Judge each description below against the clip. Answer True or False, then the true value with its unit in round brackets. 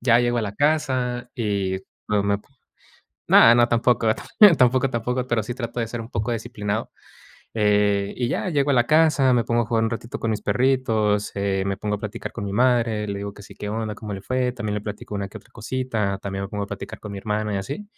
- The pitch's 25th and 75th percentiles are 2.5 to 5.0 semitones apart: True (3.1 semitones)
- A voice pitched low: True (110 Hz)